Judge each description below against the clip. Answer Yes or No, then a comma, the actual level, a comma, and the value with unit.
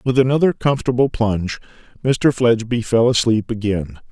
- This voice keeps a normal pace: No, slow, 130 wpm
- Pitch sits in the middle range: No, low, 115 Hz